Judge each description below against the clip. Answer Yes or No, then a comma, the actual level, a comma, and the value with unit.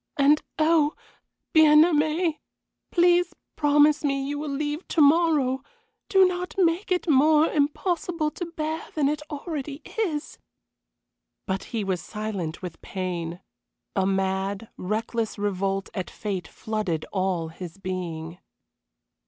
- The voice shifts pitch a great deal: Yes, wide, 8.4 semitones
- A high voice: Yes, very high, 280 Hz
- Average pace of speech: No, slow, 125 wpm